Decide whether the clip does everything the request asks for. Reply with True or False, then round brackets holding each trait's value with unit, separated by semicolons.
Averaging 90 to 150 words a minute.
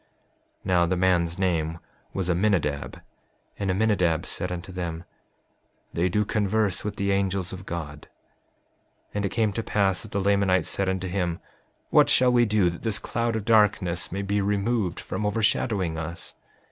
False (170 wpm)